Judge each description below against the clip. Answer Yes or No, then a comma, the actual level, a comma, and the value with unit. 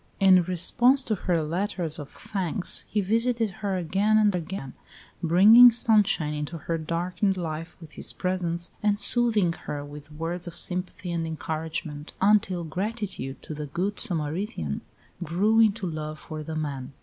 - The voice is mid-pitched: Yes, medium, 175 Hz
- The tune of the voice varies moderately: Yes, average, 4.6 semitones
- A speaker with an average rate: Yes, average, 150 wpm